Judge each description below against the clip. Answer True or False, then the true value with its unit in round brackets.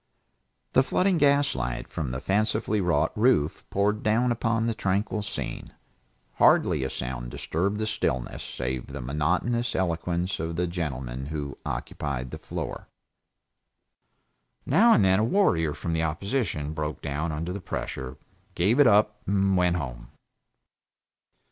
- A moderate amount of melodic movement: False (6.8 semitones)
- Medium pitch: False (90 Hz)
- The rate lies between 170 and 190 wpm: False (140 wpm)